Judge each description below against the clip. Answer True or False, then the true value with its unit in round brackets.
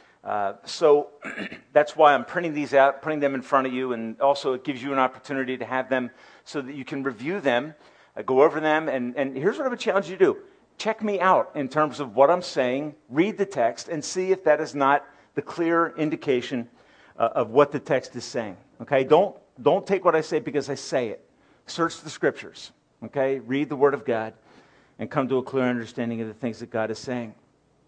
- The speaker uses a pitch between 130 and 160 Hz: True (140 Hz)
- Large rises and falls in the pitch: False (3.3 semitones)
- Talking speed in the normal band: False (225 wpm)